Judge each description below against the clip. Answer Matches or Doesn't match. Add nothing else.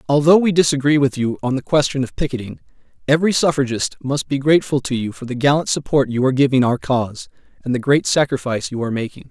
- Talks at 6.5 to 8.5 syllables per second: Matches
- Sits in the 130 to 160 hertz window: Matches